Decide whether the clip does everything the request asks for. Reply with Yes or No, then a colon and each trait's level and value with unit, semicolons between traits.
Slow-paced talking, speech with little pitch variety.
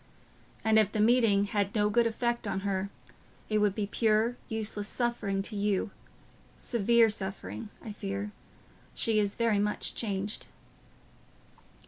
Yes: slow, 130 wpm; narrow, 2.0 semitones